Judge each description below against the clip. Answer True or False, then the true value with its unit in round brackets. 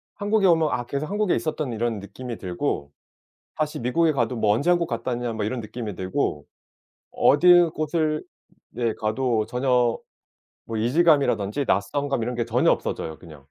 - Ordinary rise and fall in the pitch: False (5.8 semitones)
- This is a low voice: True (125 Hz)